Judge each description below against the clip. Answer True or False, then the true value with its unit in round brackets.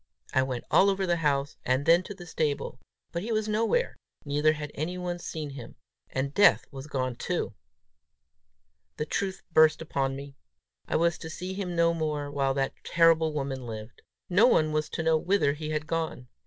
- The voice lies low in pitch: False (155 Hz)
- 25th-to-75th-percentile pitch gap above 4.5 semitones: False (3.9 semitones)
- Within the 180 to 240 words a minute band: True (185 wpm)